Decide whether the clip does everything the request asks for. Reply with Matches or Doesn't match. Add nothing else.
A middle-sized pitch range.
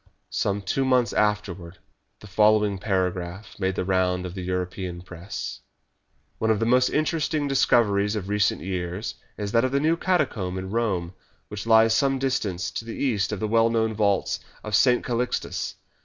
Matches